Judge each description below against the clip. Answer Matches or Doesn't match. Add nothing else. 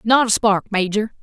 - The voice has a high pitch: Matches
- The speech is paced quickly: Doesn't match